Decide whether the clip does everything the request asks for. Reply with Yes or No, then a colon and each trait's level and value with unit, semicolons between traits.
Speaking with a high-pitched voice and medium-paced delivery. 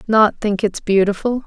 Yes: high, 210 Hz; average, 165 wpm